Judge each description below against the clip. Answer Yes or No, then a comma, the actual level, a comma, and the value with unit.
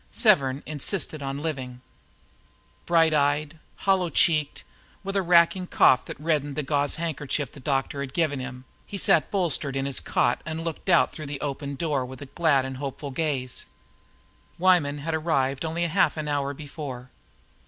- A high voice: No, medium, 145 Hz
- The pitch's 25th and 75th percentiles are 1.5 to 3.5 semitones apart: Yes, average, 3.2 semitones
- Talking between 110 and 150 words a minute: No, average, 165 wpm